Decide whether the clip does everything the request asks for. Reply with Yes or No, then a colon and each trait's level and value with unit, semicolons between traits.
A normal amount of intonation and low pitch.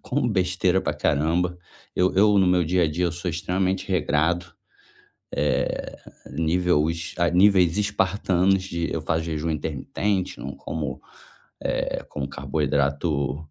Yes: average, 3.2 semitones; very low, 85 Hz